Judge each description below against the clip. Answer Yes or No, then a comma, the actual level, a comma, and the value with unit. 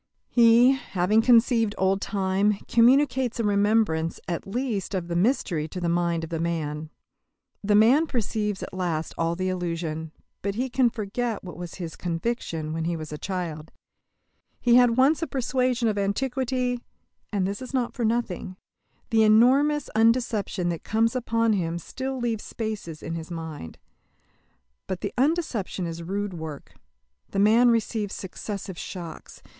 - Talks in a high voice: Yes, high, 205 Hz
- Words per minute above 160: No, average, 155 wpm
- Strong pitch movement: Yes, wide, 5.7 semitones